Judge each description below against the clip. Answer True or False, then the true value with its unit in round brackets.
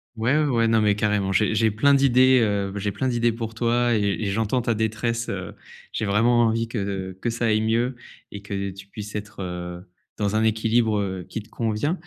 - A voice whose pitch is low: True (110 Hz)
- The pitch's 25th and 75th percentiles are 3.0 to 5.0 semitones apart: False (2.6 semitones)